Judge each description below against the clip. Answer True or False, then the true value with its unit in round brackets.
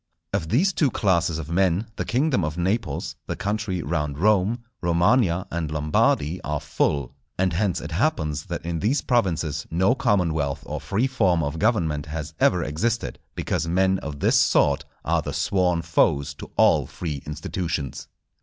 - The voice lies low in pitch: True (85 Hz)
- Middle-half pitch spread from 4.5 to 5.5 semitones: True (4.9 semitones)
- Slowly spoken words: False (165 wpm)